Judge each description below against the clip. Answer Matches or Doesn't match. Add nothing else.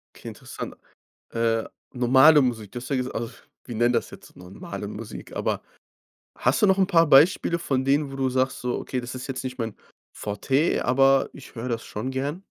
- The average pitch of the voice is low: Matches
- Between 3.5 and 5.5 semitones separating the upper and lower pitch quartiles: Doesn't match